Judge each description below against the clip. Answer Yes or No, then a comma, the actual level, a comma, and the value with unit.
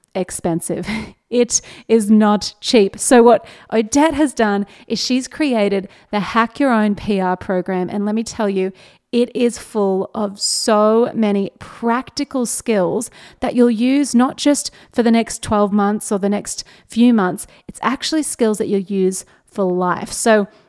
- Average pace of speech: Yes, average, 160 wpm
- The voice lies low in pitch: No, high, 215 Hz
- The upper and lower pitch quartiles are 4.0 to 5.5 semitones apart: No, average, 3.0 semitones